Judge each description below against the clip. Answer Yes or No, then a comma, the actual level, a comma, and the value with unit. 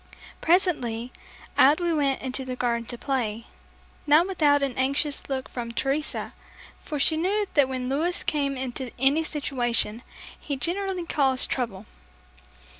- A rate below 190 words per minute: Yes, average, 140 wpm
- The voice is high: Yes, very high, 275 Hz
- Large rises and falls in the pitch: No, average, 3.5 semitones